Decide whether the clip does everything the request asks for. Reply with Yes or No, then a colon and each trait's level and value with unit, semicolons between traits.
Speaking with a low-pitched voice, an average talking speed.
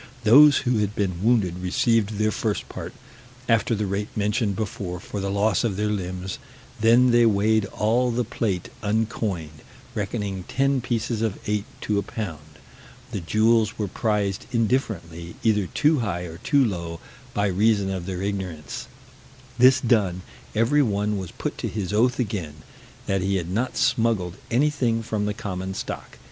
Yes: low, 105 Hz; average, 160 wpm